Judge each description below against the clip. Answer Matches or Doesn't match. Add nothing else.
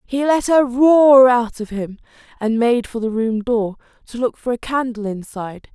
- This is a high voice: Matches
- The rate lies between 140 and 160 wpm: Doesn't match